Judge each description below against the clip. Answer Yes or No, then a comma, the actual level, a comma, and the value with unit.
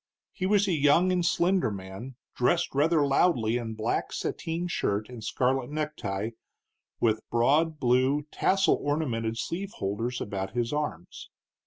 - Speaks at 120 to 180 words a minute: Yes, average, 140 wpm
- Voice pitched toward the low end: Yes, low, 130 Hz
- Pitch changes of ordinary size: No, wide, 6.4 semitones